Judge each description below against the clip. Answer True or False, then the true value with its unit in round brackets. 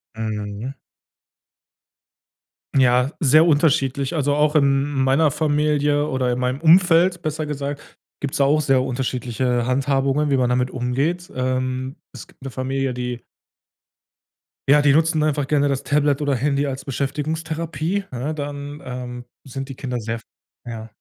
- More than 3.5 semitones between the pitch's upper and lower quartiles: False (2.7 semitones)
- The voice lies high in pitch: False (140 Hz)